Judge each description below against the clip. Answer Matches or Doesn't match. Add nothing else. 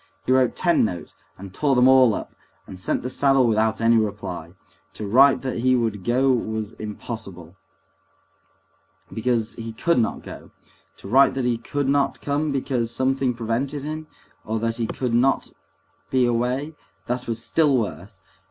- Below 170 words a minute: Matches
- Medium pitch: Doesn't match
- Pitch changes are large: Doesn't match